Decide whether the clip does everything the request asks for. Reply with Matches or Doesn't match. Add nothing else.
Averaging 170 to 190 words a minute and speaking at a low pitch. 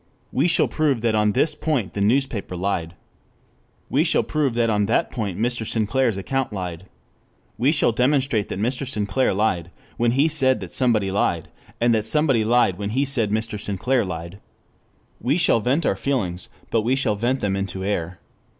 Matches